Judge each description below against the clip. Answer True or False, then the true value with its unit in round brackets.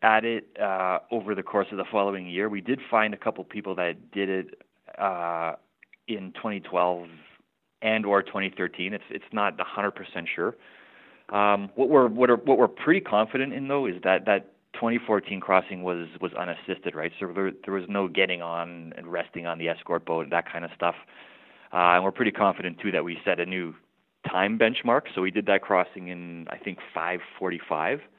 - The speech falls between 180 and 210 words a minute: True (190 wpm)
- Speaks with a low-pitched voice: True (95 Hz)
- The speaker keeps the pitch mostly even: False (3.0 semitones)